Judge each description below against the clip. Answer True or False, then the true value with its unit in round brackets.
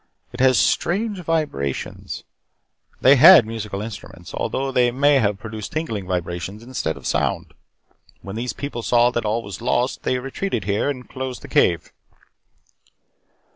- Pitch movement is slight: False (4.7 semitones)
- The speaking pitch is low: True (120 Hz)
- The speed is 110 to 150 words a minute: True (145 wpm)